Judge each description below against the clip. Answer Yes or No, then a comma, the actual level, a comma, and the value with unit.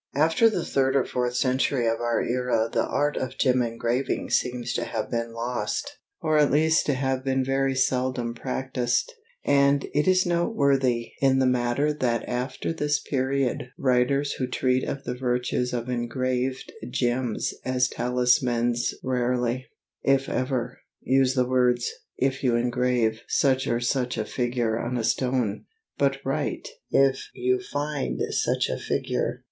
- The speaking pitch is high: No, low, 130 Hz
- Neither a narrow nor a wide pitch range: No, narrow, 1.8 semitones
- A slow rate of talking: No, average, 150 wpm